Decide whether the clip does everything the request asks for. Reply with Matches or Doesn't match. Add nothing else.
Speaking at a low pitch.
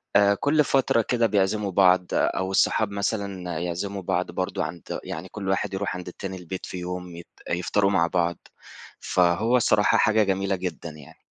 Matches